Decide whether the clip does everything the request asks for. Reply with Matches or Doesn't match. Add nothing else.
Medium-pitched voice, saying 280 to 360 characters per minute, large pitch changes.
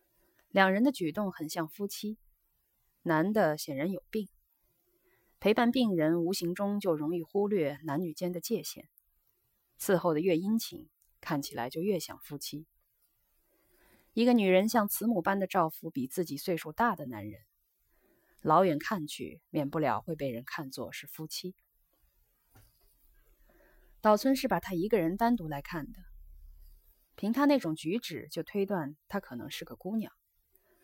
Doesn't match